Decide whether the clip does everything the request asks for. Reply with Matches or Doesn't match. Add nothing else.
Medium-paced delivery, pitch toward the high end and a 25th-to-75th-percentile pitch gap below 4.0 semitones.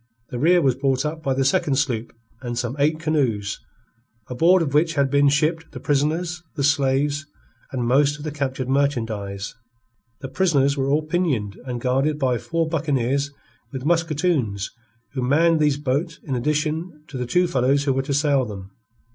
Doesn't match